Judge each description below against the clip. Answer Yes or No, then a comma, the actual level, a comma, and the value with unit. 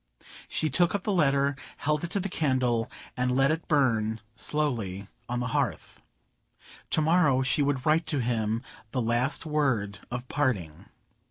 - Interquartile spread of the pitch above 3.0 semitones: Yes, average, 4.4 semitones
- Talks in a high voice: No, low, 130 Hz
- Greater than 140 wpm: Yes, average, 160 wpm